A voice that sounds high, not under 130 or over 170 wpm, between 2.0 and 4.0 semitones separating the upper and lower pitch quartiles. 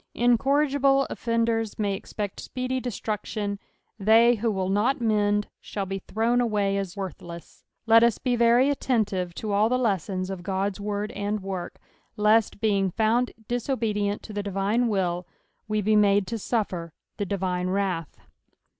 Yes: high, 210 Hz; average, 155 wpm; average, 3.0 semitones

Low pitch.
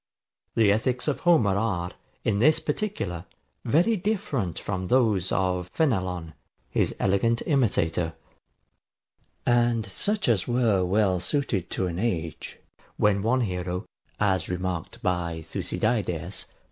Yes: low, 100 Hz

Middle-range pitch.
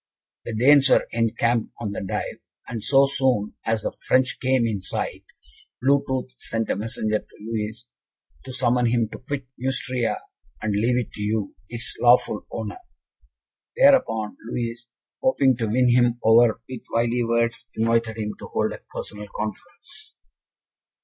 No: low, 115 Hz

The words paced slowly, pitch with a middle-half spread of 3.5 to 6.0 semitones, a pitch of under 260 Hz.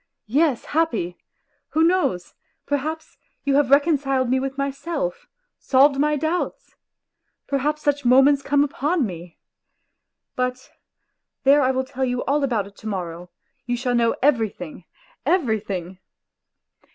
No: slow, 125 wpm; average, 3.8 semitones; very high, 270 Hz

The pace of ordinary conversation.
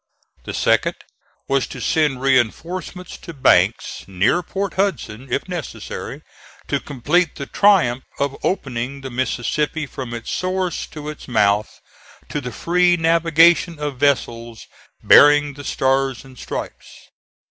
No: slow, 130 wpm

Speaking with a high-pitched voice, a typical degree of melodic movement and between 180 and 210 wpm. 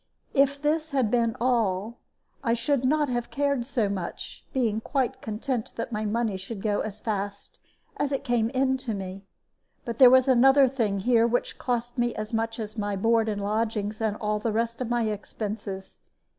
Yes: high, 230 Hz; average, 3.1 semitones; average, 185 wpm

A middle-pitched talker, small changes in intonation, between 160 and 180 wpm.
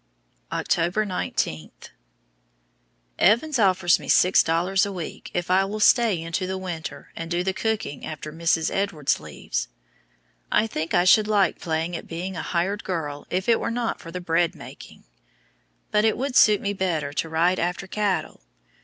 No: medium, 180 Hz; average, 3.6 semitones; average, 170 wpm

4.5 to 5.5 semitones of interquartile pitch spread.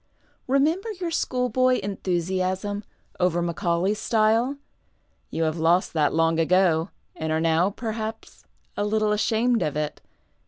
Yes: average, 5.2 semitones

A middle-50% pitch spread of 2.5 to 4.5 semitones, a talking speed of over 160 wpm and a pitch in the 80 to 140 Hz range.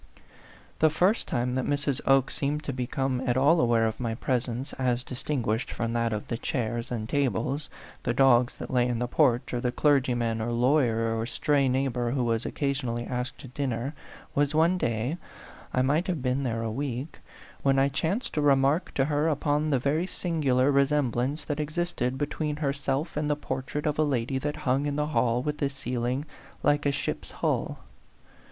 Yes: average, 3.3 semitones; average, 200 wpm; low, 135 Hz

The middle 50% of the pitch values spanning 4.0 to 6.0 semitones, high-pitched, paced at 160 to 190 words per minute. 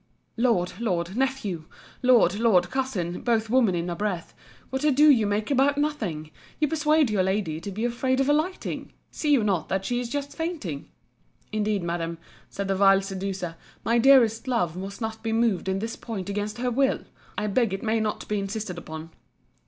Yes: average, 5.1 semitones; high, 215 Hz; average, 185 wpm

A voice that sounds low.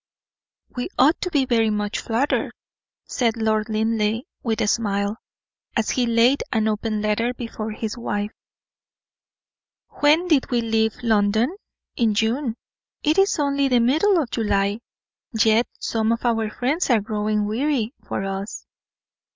No: high, 225 Hz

